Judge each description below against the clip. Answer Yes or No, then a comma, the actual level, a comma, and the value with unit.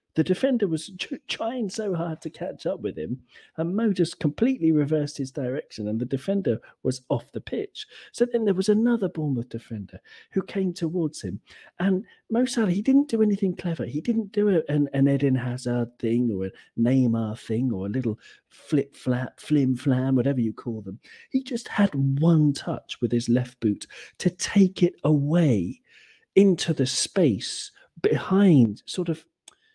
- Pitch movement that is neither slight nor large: No, wide, 7.6 semitones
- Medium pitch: Yes, medium, 155 Hz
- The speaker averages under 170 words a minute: No, average, 175 wpm